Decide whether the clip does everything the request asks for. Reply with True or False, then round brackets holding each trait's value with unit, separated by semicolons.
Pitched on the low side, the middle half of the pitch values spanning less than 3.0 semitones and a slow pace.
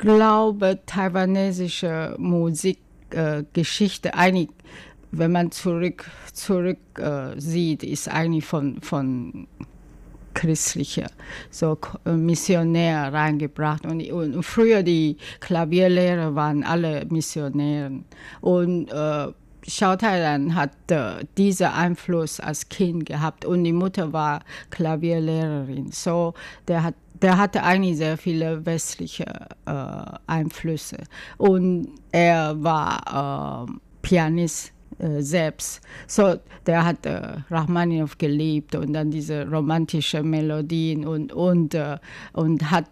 False (165 Hz; 2.5 semitones; 105 wpm)